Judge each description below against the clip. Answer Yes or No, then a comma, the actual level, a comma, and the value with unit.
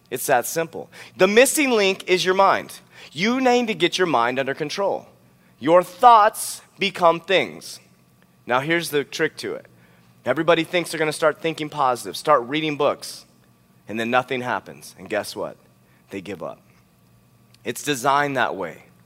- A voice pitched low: No, medium, 150 Hz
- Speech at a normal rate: Yes, average, 165 wpm